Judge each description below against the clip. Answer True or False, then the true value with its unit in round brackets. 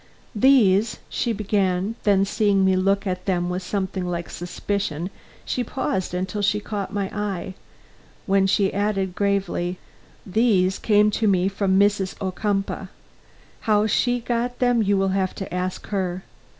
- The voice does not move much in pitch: True (1.9 semitones)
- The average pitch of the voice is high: True (195 Hz)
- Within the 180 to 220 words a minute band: False (150 wpm)